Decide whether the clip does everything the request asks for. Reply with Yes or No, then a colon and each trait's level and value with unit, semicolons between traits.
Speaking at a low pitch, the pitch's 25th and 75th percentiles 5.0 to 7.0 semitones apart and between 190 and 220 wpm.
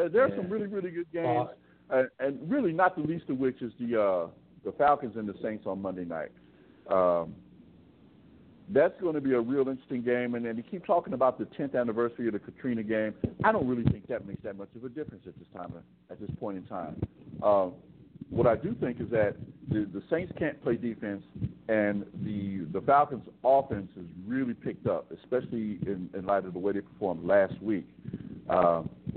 Yes: low, 120 Hz; wide, 5.4 semitones; fast, 205 wpm